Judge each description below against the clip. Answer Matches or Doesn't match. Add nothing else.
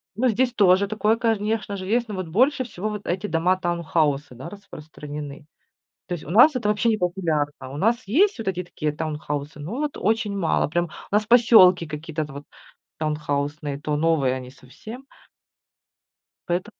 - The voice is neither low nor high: Matches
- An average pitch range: Doesn't match